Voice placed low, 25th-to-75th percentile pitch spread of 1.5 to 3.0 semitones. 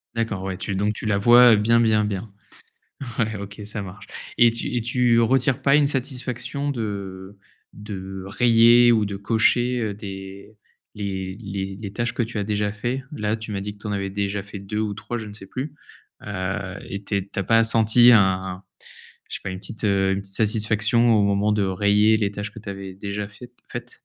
Yes: low, 105 Hz; average, 2.7 semitones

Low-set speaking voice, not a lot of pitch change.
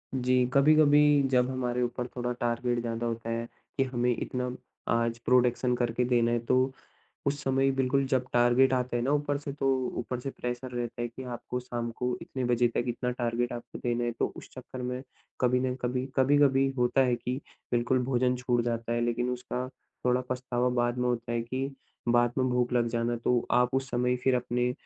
Yes: low, 125 Hz; narrow, 1.1 semitones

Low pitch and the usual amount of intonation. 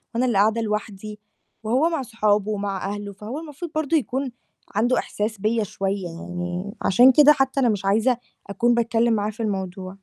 No: high, 215 Hz; average, 3.7 semitones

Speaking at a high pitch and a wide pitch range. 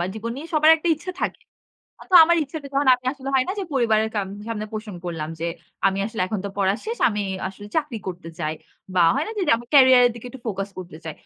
Yes: high, 230 Hz; wide, 6.3 semitones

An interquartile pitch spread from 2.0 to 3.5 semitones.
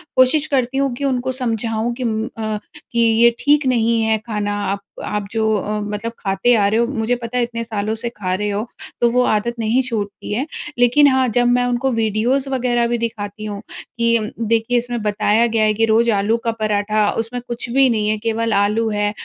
Yes: narrow, 2.4 semitones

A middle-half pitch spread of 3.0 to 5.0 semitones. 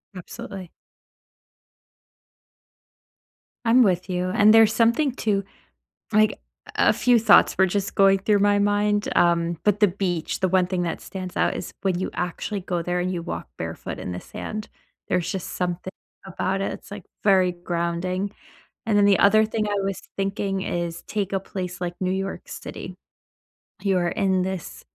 No: narrow, 2.4 semitones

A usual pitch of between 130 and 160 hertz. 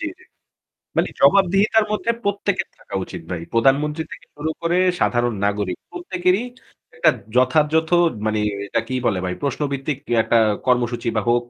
Yes: medium, 140 Hz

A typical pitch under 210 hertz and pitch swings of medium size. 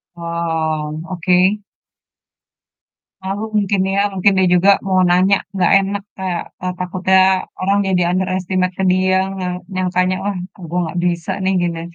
No: medium, 185 Hz; narrow, 1.4 semitones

